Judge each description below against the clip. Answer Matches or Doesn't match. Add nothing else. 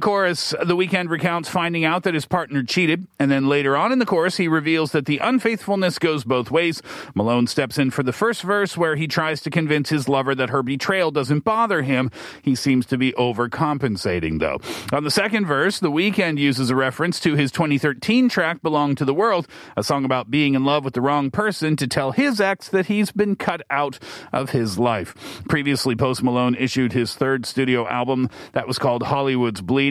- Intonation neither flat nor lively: Matches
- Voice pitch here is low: Doesn't match